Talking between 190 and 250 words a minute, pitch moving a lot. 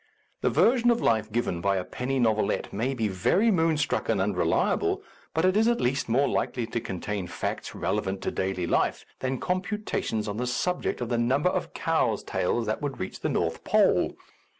Yes: average, 195 wpm; wide, 7.4 semitones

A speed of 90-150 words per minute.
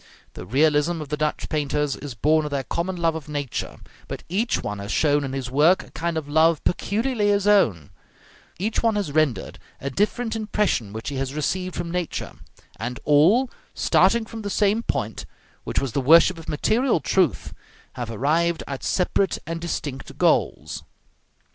No: average, 175 wpm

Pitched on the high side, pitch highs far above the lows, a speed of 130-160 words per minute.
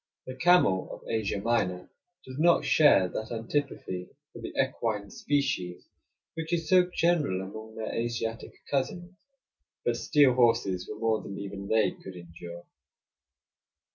No: low, 115 Hz; wide, 6.8 semitones; average, 140 wpm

